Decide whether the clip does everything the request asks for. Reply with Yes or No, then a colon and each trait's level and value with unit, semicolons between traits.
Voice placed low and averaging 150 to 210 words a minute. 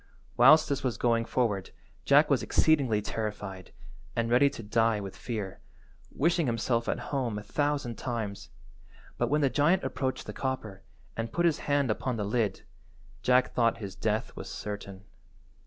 Yes: low, 115 Hz; average, 160 wpm